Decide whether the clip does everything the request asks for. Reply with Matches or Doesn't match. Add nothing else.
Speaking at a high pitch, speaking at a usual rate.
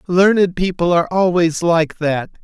Doesn't match